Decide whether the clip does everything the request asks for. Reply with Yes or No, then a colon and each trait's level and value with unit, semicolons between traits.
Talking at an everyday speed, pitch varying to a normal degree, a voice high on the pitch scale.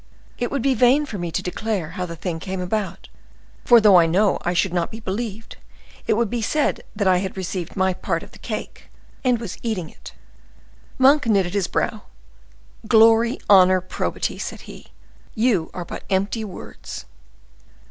Yes: average, 175 wpm; average, 4.1 semitones; high, 195 Hz